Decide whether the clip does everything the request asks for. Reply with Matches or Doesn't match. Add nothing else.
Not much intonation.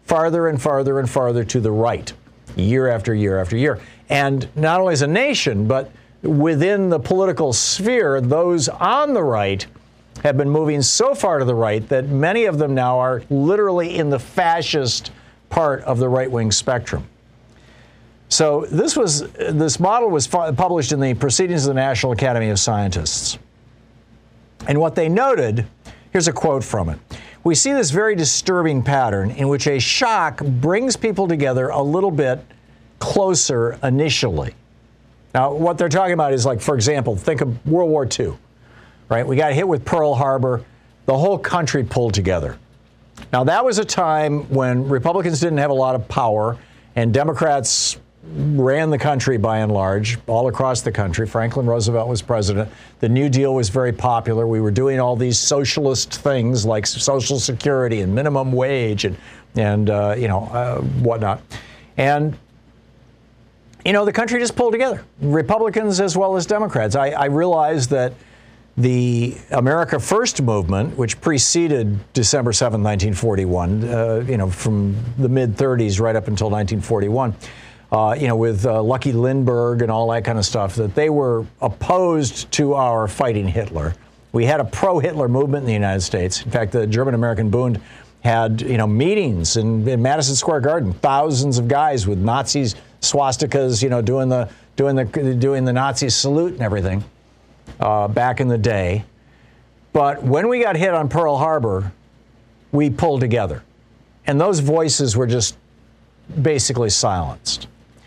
Doesn't match